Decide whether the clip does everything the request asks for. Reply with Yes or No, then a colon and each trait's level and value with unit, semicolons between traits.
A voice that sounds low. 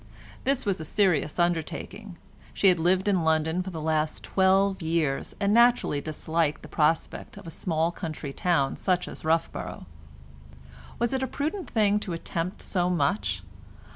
No: medium, 175 Hz